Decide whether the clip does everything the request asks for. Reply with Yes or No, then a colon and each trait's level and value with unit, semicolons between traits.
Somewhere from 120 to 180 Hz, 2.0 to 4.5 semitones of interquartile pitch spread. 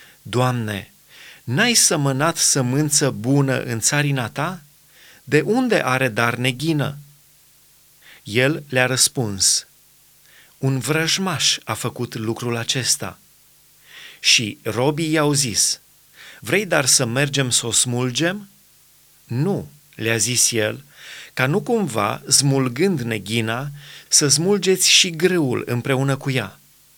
Yes: medium, 140 Hz; average, 4.0 semitones